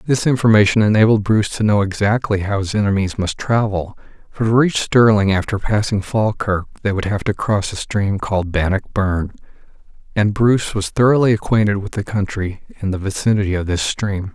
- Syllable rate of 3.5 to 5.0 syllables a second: No, 5.4 syllables/s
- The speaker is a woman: No, male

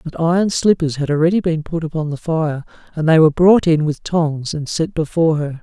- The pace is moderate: No, fast, 225 wpm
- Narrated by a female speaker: No, male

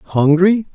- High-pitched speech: No, medium, 175 Hz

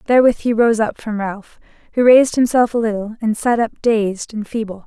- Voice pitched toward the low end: No, high, 225 Hz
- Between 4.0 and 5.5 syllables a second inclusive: Yes, 5.4 syllables/s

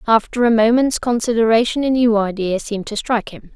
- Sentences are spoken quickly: No, average, 185 wpm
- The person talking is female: Yes, female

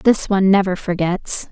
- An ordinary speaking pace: Yes, average, 160 wpm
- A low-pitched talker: No, high, 190 Hz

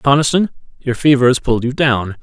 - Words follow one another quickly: No, average, 190 wpm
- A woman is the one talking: No, male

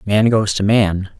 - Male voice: Yes, male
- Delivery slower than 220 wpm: Yes, average, 200 wpm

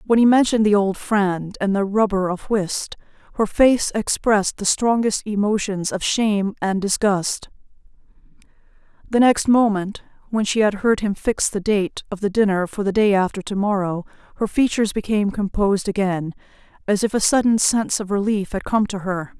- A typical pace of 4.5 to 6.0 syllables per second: No, 4.2 syllables/s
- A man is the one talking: No, female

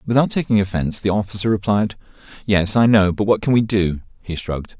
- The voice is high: No, low, 100 Hz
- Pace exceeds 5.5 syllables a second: Yes, 6.0 syllables/s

